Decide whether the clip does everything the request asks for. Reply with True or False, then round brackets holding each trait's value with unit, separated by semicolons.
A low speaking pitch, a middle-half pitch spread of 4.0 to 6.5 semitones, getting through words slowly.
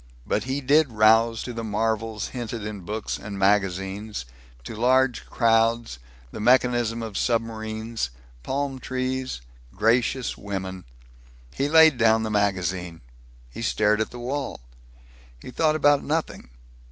False (115 Hz; 3.6 semitones; 130 wpm)